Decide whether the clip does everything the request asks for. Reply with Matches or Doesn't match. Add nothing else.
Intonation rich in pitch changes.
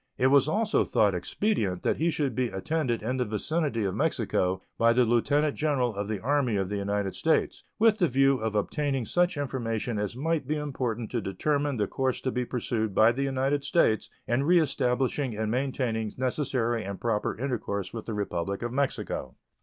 Doesn't match